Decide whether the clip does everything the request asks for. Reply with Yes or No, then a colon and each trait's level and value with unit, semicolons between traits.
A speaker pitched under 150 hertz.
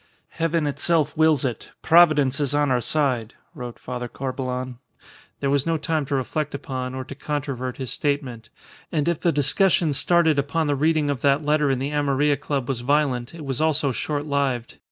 Yes: medium, 140 Hz